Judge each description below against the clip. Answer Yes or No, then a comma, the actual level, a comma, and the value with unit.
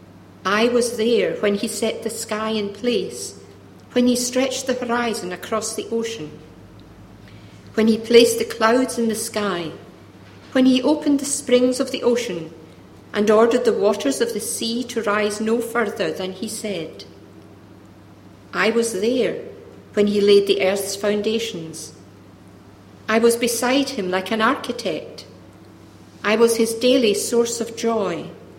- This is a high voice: Yes, high, 220 Hz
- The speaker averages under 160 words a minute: Yes, average, 150 wpm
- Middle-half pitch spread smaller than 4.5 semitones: No, average, 5.3 semitones